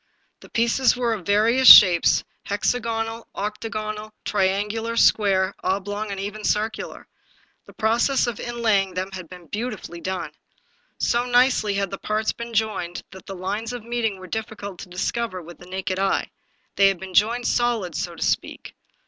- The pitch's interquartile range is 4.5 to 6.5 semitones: No, average, 3.2 semitones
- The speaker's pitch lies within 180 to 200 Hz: No, high, 210 Hz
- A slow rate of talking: No, average, 165 wpm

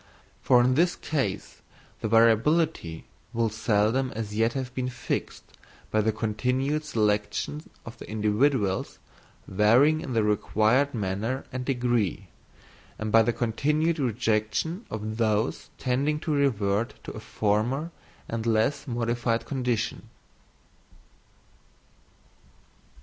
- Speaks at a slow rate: Yes, slow, 115 wpm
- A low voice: Yes, low, 115 Hz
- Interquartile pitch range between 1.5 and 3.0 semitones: No, average, 3.7 semitones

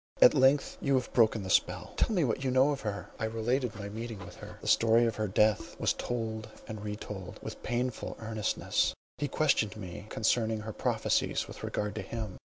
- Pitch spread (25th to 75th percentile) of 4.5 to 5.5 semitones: No, average, 2.9 semitones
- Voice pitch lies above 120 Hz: No, low, 110 Hz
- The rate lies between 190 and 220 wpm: Yes, fast, 205 wpm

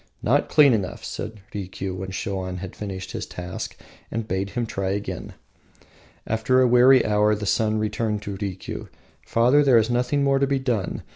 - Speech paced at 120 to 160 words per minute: No, average, 175 wpm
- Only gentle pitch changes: No, average, 4.2 semitones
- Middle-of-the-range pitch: No, low, 105 Hz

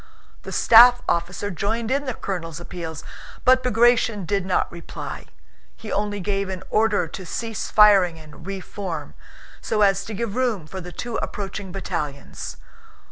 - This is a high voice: Yes, high, 200 Hz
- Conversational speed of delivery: Yes, average, 155 wpm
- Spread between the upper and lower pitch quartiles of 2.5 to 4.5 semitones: Yes, average, 3.9 semitones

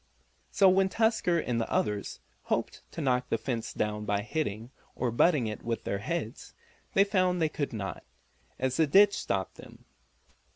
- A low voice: Yes, low, 125 Hz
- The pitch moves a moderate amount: No, wide, 8.5 semitones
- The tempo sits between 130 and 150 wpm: No, average, 170 wpm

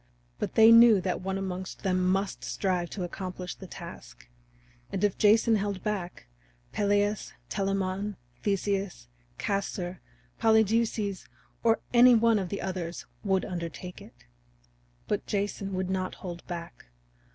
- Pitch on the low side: No, high, 195 Hz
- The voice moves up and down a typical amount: No, narrow, 2.2 semitones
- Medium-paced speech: No, slow, 130 wpm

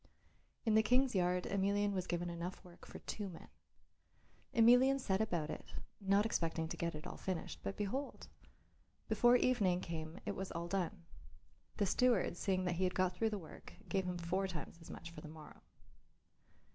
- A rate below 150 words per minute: No, average, 185 wpm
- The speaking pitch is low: No, medium, 185 Hz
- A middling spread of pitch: Yes, average, 3.4 semitones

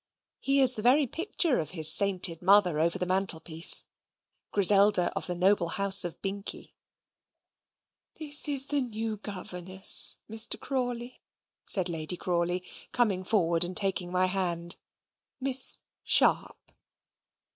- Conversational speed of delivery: No, slow, 125 wpm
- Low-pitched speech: No, high, 195 Hz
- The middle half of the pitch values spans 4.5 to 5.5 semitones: Yes, average, 4.8 semitones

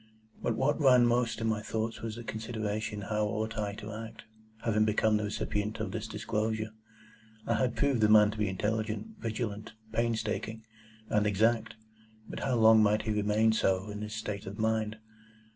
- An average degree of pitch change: No, narrow, 1.0 semitones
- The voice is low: Yes, low, 110 Hz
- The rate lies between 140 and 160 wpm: No, average, 175 wpm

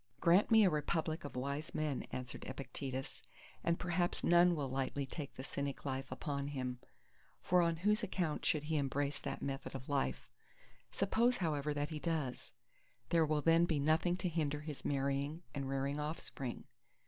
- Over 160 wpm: Yes, average, 170 wpm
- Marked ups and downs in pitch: No, average, 3.5 semitones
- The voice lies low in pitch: No, medium, 150 Hz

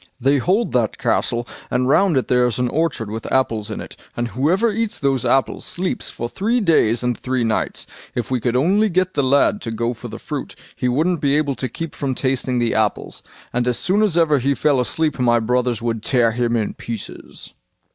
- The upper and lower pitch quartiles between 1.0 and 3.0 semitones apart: No, average, 4.6 semitones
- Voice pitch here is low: Yes, low, 130 Hz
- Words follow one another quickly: Yes, fast, 215 wpm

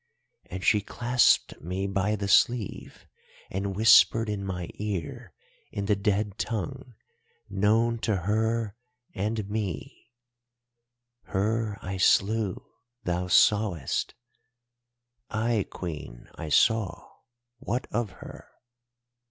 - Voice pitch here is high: No, low, 105 Hz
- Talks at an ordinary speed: No, slow, 95 wpm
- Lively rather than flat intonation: No, average, 3.4 semitones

